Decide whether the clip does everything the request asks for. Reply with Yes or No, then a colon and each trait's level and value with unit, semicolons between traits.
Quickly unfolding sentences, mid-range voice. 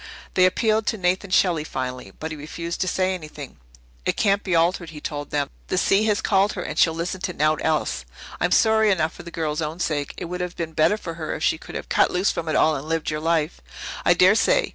Yes: fast, 250 wpm; medium, 170 Hz